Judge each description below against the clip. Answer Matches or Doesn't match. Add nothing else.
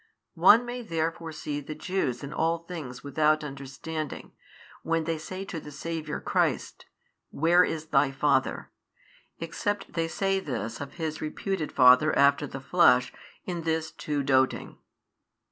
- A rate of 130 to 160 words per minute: Matches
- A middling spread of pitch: Matches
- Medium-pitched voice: Matches